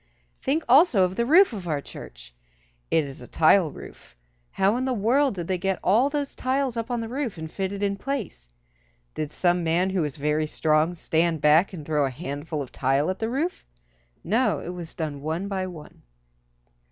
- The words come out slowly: No, average, 200 wpm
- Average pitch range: No, wide, 6.9 semitones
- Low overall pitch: No, medium, 180 Hz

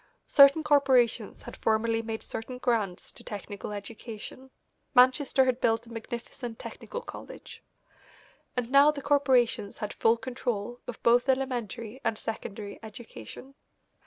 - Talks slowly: Yes, slow, 130 wpm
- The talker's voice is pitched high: Yes, high, 235 Hz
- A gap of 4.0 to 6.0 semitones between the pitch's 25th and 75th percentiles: No, average, 2.9 semitones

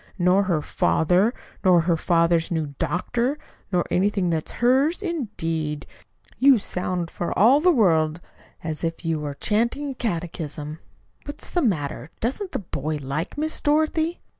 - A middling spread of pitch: No, wide, 7.5 semitones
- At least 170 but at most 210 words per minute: No, average, 150 wpm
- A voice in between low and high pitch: Yes, medium, 180 Hz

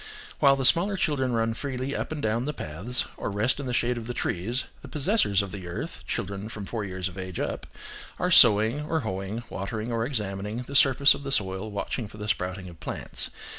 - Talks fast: Yes, fast, 215 wpm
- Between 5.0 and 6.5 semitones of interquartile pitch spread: Yes, average, 5.3 semitones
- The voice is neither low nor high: No, low, 115 Hz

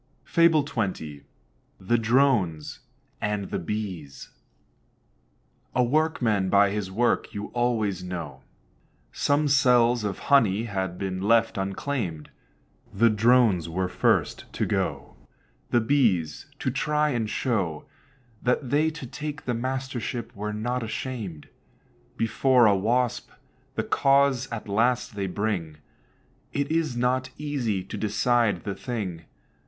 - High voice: No, low, 115 Hz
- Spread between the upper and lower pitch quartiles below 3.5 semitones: No, average, 4.9 semitones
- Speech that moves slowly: Yes, slow, 125 wpm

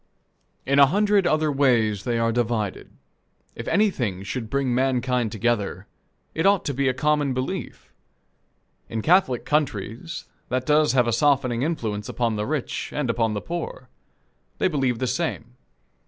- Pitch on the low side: Yes, low, 130 Hz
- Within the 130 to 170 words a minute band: Yes, average, 155 wpm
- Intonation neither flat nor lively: Yes, average, 4.6 semitones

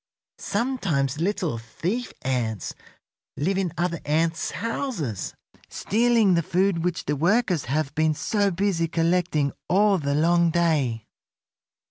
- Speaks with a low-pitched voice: No, medium, 170 Hz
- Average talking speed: No, slow, 120 wpm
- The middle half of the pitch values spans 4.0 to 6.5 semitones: Yes, average, 4.9 semitones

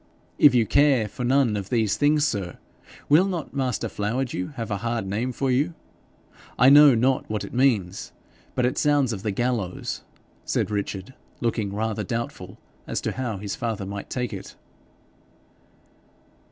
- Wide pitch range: No, average, 4.4 semitones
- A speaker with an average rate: Yes, average, 160 wpm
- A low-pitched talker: Yes, low, 120 Hz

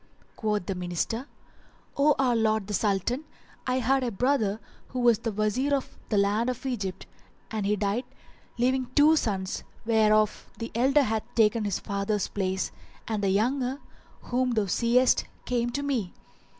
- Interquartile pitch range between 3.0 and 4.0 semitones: Yes, average, 3.7 semitones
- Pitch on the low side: No, high, 225 Hz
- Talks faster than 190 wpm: No, average, 155 wpm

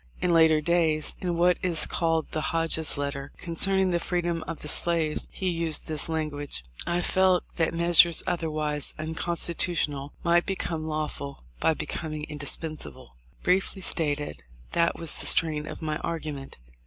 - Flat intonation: Yes, narrow, 2.1 semitones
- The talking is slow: No, average, 145 wpm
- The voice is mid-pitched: Yes, medium, 160 Hz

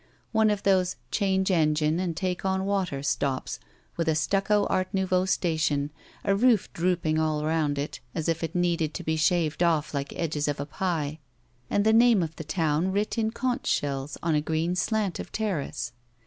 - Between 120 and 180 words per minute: No, average, 190 wpm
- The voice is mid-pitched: Yes, medium, 170 Hz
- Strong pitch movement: No, average, 3.8 semitones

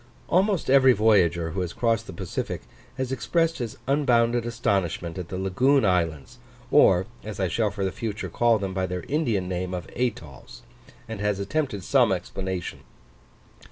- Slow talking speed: No, average, 160 wpm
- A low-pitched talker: Yes, low, 105 Hz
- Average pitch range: Yes, average, 4.9 semitones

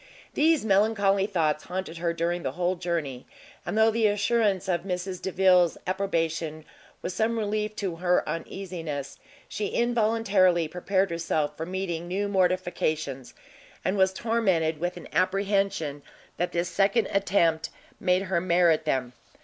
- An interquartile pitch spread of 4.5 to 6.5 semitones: No, average, 3.0 semitones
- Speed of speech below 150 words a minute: Yes, average, 140 wpm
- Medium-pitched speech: Yes, medium, 180 Hz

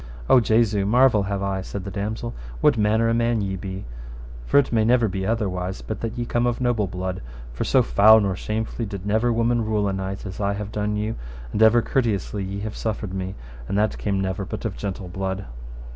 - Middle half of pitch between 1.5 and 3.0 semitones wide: Yes, average, 2.7 semitones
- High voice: No, low, 105 Hz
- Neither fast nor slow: No, fast, 230 wpm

